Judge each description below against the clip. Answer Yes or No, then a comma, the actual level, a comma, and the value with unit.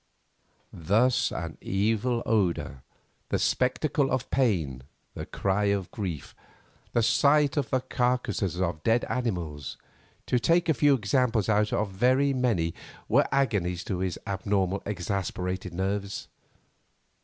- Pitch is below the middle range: Yes, low, 105 Hz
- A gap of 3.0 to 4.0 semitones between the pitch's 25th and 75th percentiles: No, wide, 5.4 semitones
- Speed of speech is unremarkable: No, slow, 125 wpm